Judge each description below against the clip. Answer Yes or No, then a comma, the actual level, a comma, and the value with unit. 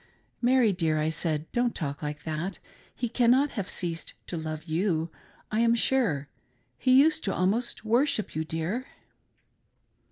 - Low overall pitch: No, high, 190 Hz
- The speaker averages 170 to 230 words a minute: No, average, 155 wpm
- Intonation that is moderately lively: No, wide, 7.2 semitones